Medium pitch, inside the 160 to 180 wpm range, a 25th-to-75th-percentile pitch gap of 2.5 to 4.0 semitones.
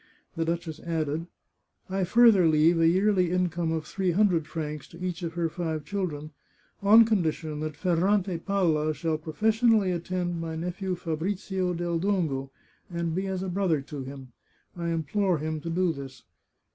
Yes: medium, 170 Hz; average, 170 wpm; average, 2.9 semitones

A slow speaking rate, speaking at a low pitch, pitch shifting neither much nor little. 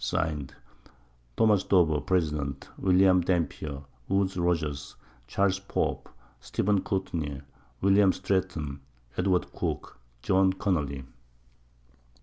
Yes: slow, 95 wpm; very low, 90 Hz; average, 4.2 semitones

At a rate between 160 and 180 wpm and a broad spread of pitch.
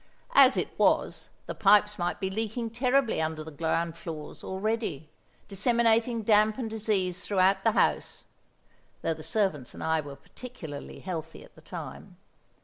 No: average, 150 wpm; wide, 5.7 semitones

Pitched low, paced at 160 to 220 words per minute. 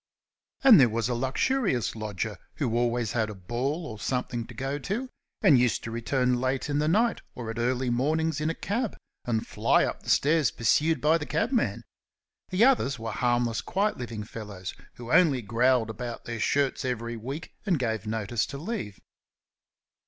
Yes: low, 125 Hz; average, 180 wpm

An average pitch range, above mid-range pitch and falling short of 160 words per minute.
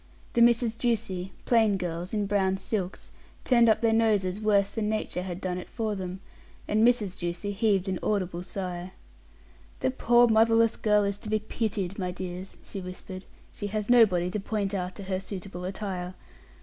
No: average, 3.0 semitones; high, 200 Hz; average, 175 wpm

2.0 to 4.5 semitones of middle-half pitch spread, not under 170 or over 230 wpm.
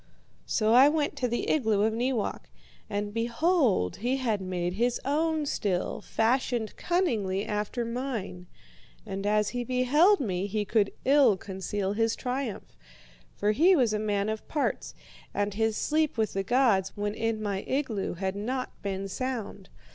No: average, 4.2 semitones; average, 155 wpm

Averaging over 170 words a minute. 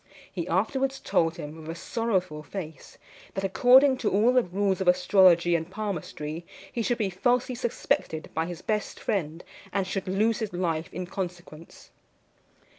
No: average, 160 wpm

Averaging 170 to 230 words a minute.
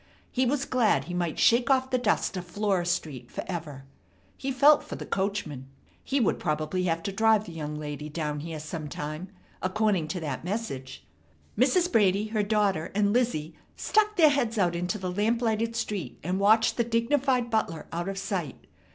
Yes: average, 175 wpm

